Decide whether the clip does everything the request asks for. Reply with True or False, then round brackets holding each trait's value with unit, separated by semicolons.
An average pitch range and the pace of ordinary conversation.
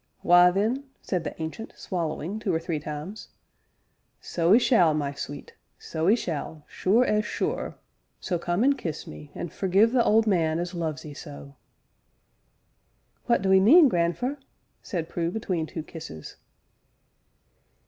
True (5.0 semitones; 150 wpm)